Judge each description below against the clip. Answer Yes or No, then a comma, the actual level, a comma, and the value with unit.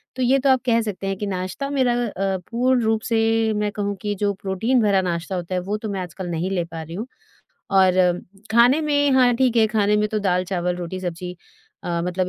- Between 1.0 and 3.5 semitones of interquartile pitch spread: No, average, 4.3 semitones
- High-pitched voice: Yes, high, 205 Hz